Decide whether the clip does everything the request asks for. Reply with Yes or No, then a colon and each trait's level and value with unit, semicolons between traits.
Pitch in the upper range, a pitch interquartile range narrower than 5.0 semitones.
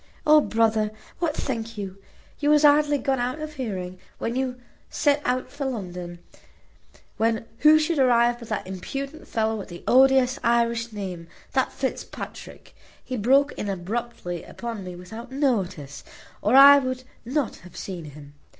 No: high, 235 Hz; wide, 5.5 semitones